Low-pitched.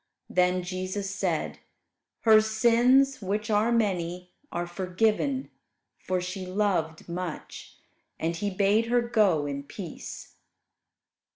No: high, 195 Hz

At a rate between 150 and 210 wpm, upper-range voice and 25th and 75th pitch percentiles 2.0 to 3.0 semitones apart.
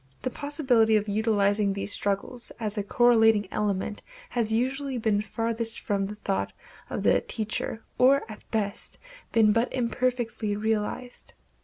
No: average, 140 wpm; high, 220 Hz; narrow, 2.6 semitones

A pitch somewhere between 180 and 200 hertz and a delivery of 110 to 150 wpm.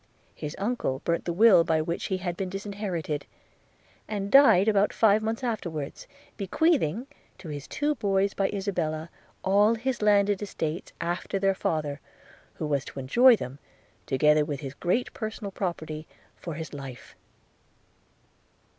Yes: high, 190 Hz; average, 145 wpm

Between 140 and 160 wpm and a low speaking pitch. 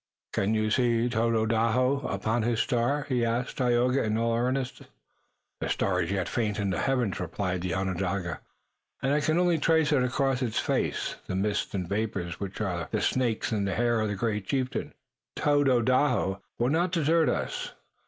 No: average, 175 wpm; low, 115 Hz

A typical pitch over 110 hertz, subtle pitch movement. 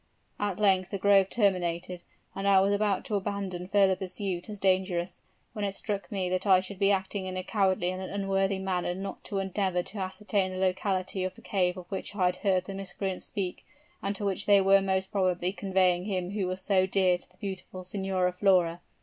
Yes: high, 190 Hz; narrow, 1.3 semitones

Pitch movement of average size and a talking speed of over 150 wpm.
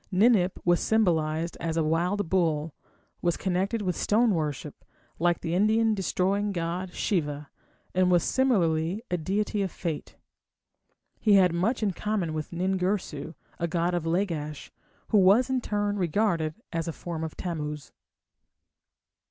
No: average, 3.8 semitones; average, 145 wpm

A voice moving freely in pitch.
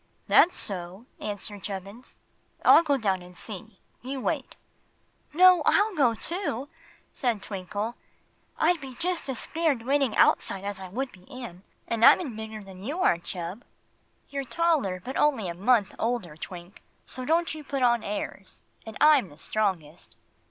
Yes: wide, 6.5 semitones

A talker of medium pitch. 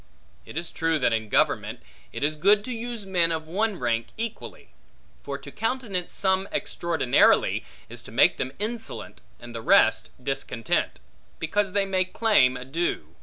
Yes: medium, 175 Hz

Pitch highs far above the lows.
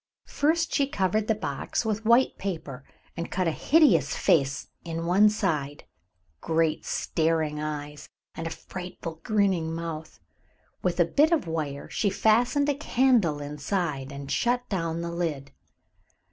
Yes: wide, 5.9 semitones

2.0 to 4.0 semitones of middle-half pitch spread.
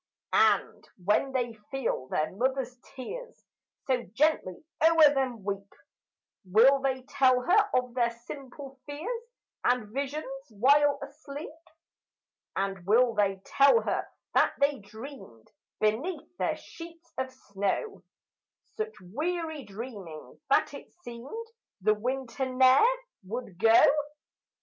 No: average, 4.8 semitones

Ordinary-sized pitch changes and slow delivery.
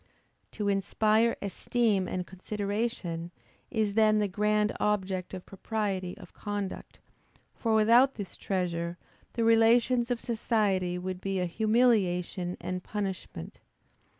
Yes: average, 3.2 semitones; slow, 120 wpm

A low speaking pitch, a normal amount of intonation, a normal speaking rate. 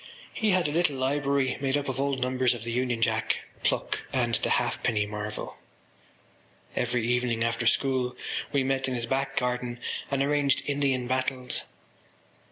No: low, 130 Hz; narrow, 2.3 semitones; average, 160 wpm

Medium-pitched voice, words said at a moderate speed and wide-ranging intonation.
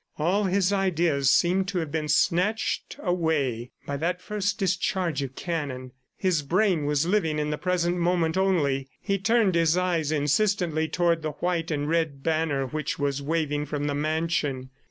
No: medium, 165 Hz; average, 165 wpm; average, 3.7 semitones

